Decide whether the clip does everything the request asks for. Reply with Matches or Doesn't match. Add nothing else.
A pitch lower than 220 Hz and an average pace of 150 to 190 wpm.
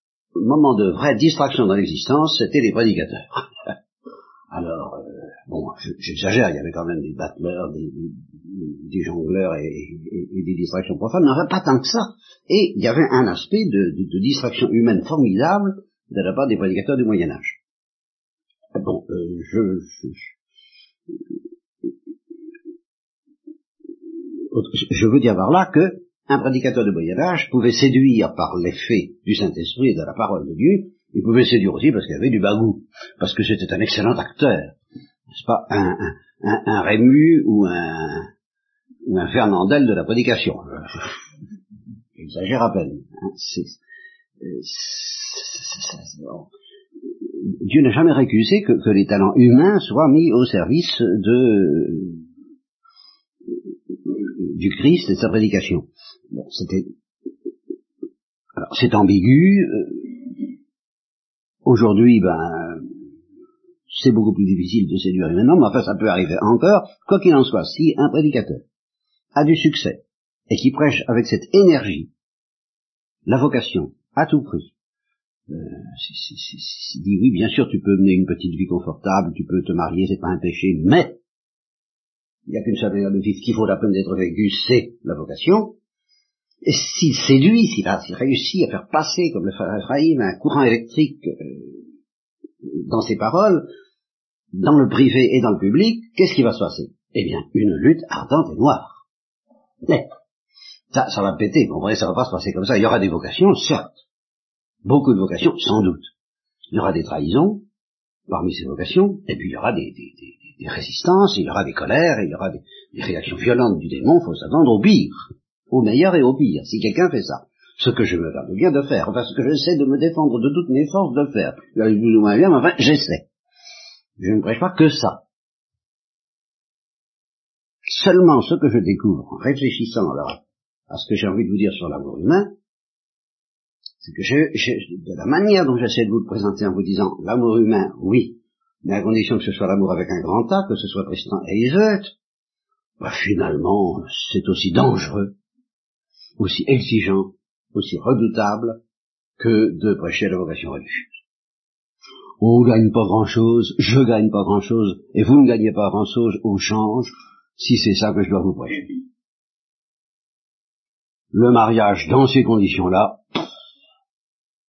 Matches